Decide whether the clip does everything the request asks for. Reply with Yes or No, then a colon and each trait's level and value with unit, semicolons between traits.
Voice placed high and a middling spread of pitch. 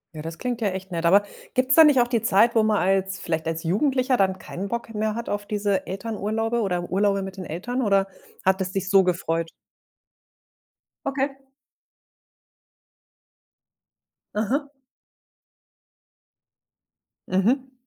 Yes: high, 200 Hz; average, 3.9 semitones